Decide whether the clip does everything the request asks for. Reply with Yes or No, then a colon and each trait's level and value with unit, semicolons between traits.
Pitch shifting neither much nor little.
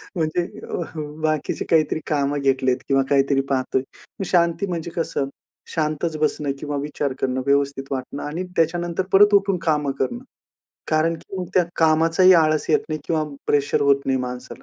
Yes: average, 3.2 semitones